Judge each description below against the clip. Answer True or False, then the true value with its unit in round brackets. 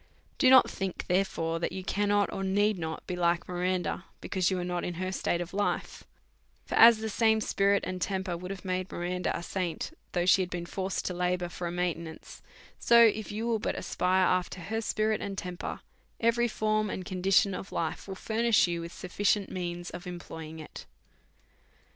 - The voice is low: False (185 Hz)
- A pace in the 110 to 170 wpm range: False (200 wpm)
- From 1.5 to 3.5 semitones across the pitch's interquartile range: True (2.7 semitones)